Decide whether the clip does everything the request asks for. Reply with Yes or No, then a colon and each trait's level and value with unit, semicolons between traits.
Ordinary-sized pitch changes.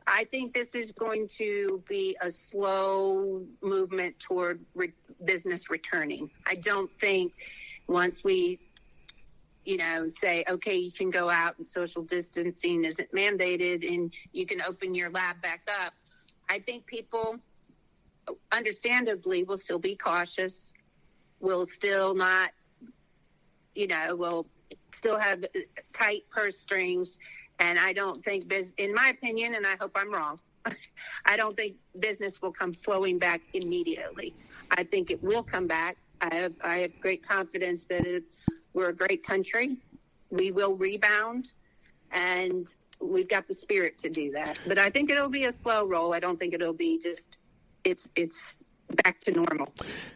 Yes: average, 4.2 semitones